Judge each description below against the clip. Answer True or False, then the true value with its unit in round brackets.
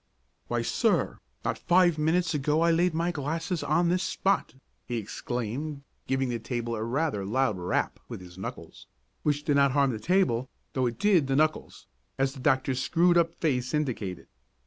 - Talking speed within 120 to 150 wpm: False (175 wpm)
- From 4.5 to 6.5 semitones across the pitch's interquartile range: True (5.2 semitones)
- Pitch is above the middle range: False (140 Hz)